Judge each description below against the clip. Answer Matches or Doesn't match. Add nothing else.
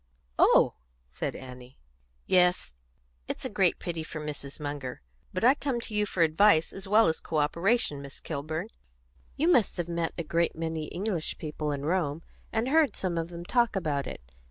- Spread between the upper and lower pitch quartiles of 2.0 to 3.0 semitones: Doesn't match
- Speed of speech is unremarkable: Matches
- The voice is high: Doesn't match